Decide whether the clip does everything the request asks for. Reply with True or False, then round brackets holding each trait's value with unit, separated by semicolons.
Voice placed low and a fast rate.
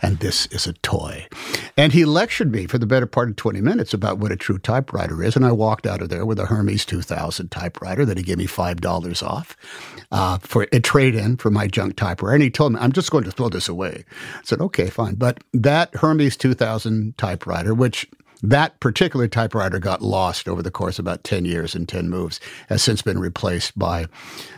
True (110 Hz; 220 wpm)